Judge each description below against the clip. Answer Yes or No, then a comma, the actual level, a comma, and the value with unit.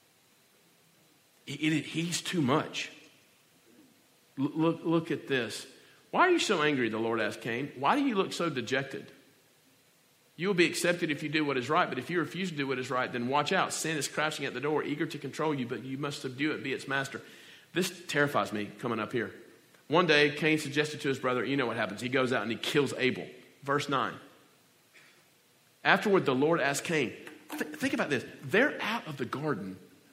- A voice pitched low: No, medium, 145 Hz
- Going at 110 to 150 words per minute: No, average, 200 wpm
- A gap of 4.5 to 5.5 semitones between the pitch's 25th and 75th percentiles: No, average, 4.0 semitones